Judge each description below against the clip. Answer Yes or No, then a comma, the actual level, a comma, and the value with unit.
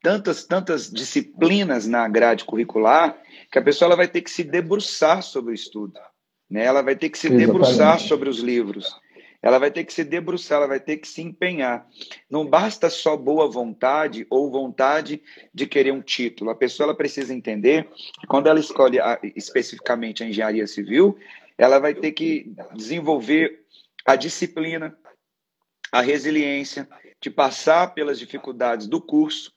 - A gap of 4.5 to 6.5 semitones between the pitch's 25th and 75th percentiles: Yes, average, 5.0 semitones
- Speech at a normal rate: Yes, average, 160 wpm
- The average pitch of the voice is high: No, medium, 145 Hz